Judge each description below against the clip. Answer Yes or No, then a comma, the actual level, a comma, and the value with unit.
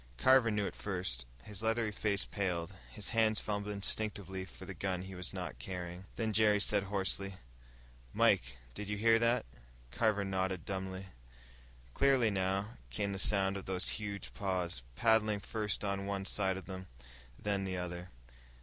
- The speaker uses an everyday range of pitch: No, narrow, 2.0 semitones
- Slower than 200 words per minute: Yes, average, 160 wpm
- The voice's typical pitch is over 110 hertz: No, low, 100 Hz